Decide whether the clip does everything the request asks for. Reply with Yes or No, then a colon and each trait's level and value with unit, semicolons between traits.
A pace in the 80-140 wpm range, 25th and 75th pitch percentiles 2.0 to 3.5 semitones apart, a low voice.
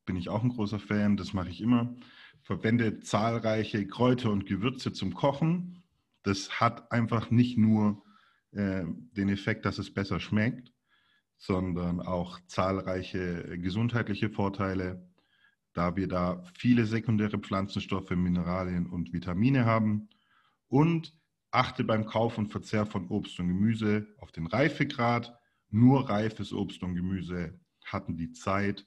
No: average, 135 wpm; average, 3.9 semitones; low, 105 Hz